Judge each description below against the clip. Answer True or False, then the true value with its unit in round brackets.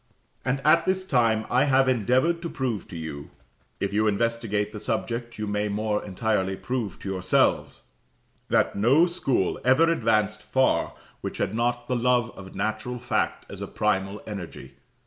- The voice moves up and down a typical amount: True (3.6 semitones)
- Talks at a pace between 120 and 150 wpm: False (165 wpm)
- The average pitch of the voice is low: True (115 Hz)